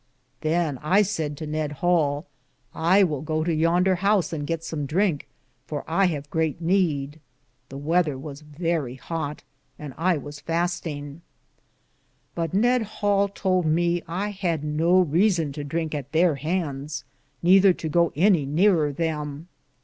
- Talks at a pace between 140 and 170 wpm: Yes, average, 155 wpm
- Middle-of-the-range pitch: Yes, medium, 165 Hz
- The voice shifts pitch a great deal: No, average, 3.3 semitones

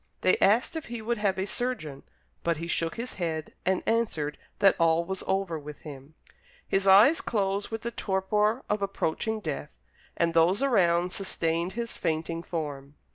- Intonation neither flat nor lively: Yes, average, 4.6 semitones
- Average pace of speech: Yes, average, 170 wpm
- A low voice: No, high, 190 Hz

